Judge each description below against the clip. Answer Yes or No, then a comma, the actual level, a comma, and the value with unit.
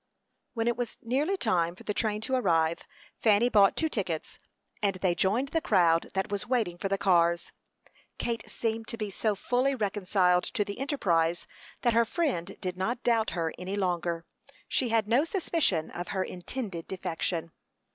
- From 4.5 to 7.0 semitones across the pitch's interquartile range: Yes, average, 5.1 semitones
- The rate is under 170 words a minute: No, average, 175 wpm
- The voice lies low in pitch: No, high, 205 Hz